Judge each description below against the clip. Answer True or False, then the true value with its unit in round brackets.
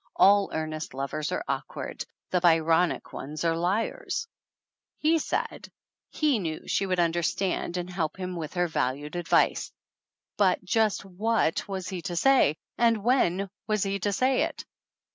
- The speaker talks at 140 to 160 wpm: True (155 wpm)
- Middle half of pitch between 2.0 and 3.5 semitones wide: False (3.9 semitones)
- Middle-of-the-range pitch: True (180 Hz)